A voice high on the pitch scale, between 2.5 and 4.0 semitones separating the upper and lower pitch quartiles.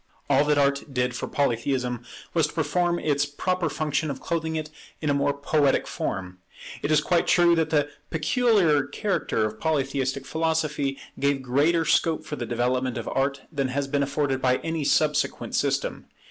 No: medium, 145 Hz; average, 2.9 semitones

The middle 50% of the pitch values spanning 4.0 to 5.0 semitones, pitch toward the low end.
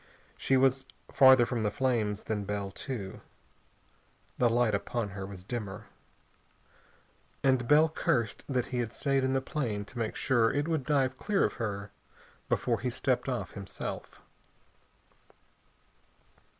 Yes: average, 4.3 semitones; low, 120 Hz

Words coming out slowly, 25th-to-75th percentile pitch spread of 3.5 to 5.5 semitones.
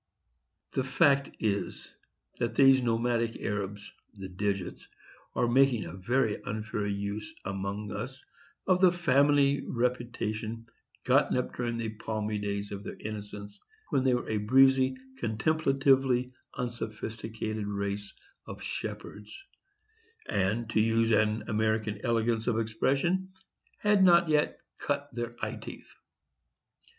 Yes: slow, 120 wpm; average, 3.9 semitones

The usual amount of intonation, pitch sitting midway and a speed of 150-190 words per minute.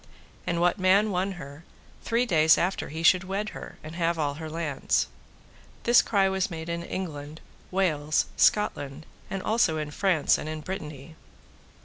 Yes: average, 3.7 semitones; medium, 170 Hz; average, 160 wpm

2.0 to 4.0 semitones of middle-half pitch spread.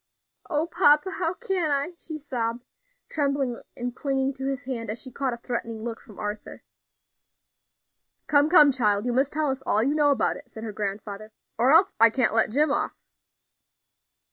No: average, 4.4 semitones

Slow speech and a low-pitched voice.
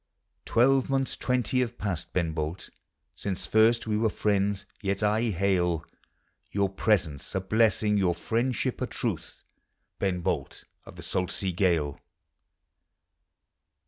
Yes: slow, 130 wpm; low, 100 Hz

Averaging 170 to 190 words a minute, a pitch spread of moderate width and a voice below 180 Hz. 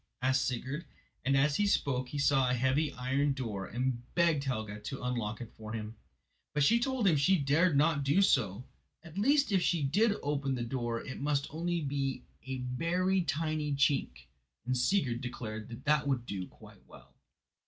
Yes: average, 180 wpm; average, 3.9 semitones; low, 135 Hz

